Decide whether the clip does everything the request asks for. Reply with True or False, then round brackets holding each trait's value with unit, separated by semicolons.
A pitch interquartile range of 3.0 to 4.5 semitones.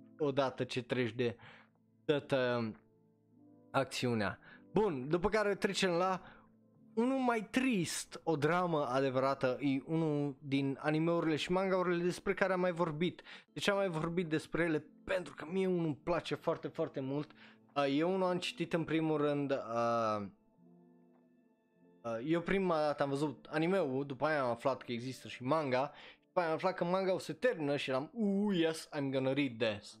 False (5.2 semitones)